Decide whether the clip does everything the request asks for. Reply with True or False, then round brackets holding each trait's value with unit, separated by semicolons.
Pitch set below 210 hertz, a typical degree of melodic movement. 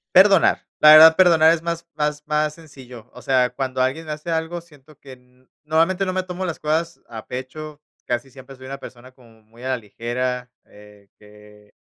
True (135 Hz; 4.4 semitones)